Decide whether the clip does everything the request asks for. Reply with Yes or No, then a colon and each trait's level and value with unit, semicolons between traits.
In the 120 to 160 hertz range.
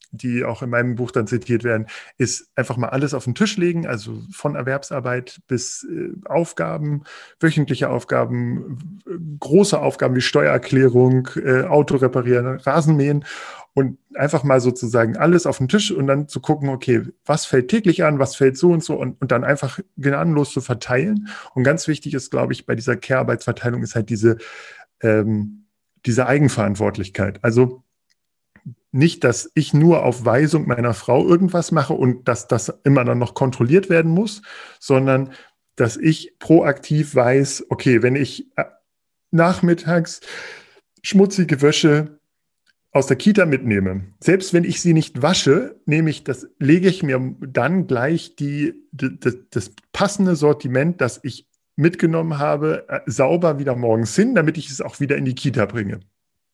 Yes: medium, 140 Hz